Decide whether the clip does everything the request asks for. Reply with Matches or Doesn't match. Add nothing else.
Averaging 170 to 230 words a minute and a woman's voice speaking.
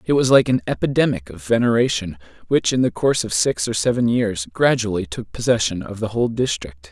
Doesn't match